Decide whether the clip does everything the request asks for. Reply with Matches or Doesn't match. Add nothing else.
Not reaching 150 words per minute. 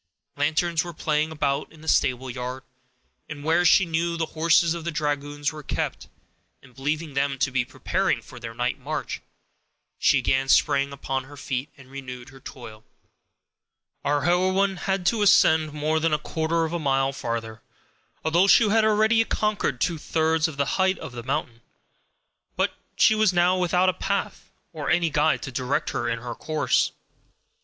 Doesn't match